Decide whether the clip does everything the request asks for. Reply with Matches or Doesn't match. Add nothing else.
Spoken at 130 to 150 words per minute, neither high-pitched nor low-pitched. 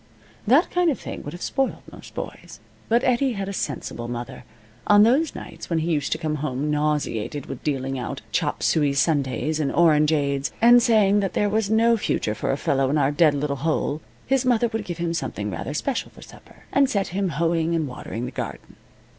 Doesn't match